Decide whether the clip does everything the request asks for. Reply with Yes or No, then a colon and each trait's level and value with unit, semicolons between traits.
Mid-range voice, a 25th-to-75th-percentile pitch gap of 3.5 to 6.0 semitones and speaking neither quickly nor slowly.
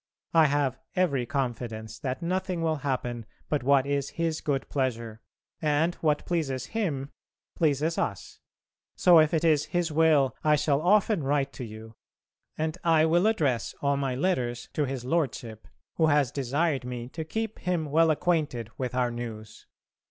Yes: medium, 145 Hz; average, 4.2 semitones; average, 160 wpm